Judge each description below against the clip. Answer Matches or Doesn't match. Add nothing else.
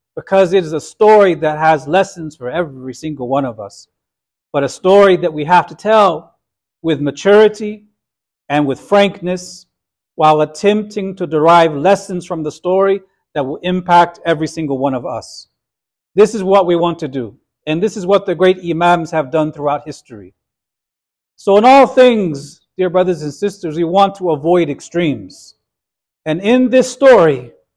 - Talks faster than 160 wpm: Matches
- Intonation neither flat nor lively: Matches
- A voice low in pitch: Doesn't match